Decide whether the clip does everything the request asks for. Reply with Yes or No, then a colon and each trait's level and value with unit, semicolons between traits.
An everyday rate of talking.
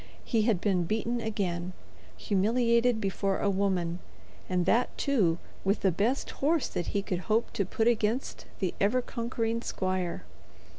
Yes: average, 150 wpm